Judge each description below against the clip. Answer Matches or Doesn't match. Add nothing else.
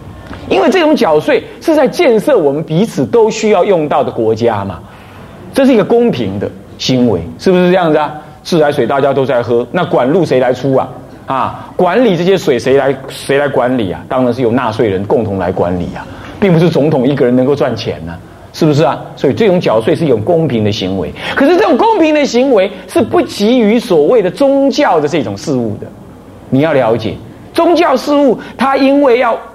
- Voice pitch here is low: Doesn't match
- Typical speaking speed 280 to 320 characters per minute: Matches